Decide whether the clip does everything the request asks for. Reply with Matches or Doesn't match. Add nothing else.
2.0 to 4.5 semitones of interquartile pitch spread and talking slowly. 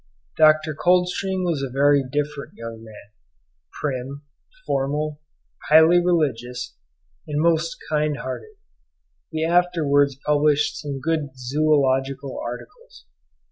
Matches